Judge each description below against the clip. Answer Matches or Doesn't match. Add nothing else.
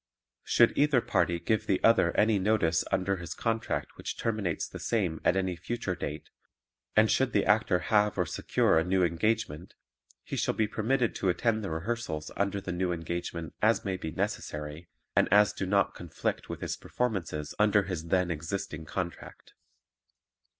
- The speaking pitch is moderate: Doesn't match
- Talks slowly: Doesn't match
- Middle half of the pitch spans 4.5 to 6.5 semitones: Doesn't match